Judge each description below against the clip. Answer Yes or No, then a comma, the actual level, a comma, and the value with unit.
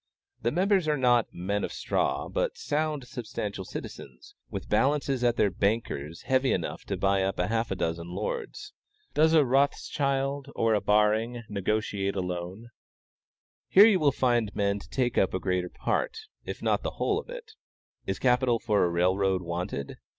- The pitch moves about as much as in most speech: No, wide, 6.1 semitones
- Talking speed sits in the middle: Yes, average, 170 wpm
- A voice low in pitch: Yes, low, 110 Hz